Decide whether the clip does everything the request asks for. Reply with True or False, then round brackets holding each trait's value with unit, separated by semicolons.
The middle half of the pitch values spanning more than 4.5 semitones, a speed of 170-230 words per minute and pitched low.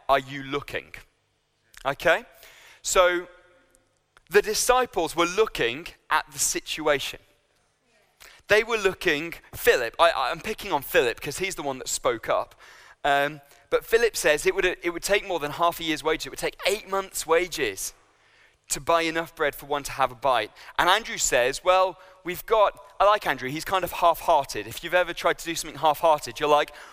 False (4.9 semitones; 185 wpm; 175 Hz)